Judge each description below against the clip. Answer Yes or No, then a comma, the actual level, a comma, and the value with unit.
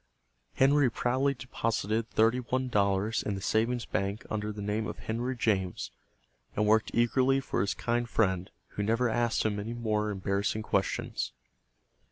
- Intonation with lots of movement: No, narrow, 2.6 semitones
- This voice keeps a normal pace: Yes, average, 155 wpm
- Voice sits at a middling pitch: No, low, 110 Hz